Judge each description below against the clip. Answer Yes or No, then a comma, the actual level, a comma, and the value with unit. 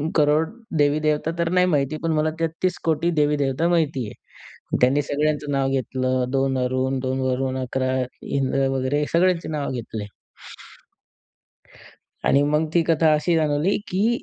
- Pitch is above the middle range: No, medium, 145 Hz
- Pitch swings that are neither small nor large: Yes, average, 3.4 semitones